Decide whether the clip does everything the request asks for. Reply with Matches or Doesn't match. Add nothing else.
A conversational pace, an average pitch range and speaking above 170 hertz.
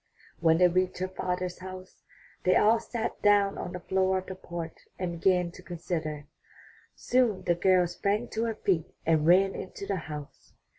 Doesn't match